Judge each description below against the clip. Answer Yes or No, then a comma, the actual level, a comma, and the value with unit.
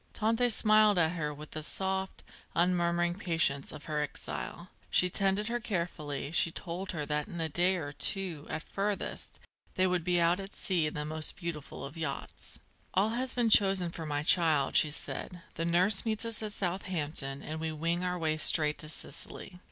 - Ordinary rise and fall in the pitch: Yes, average, 3.7 semitones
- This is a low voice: No, medium, 170 Hz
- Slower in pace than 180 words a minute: No, average, 190 wpm